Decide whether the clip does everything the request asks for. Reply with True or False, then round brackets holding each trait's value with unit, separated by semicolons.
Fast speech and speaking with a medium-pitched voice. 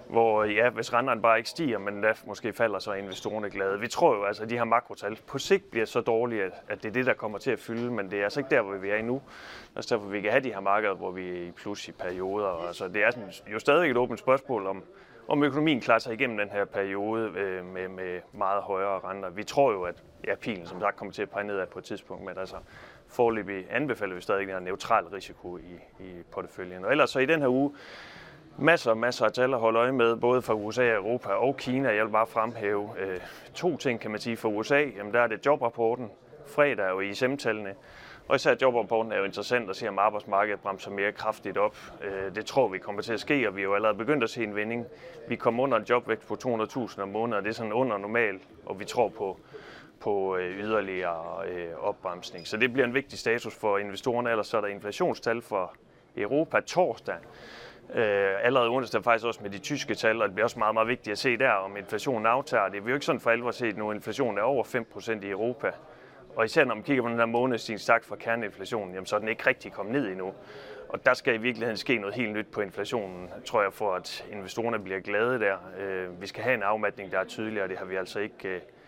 False (245 wpm; 110 Hz)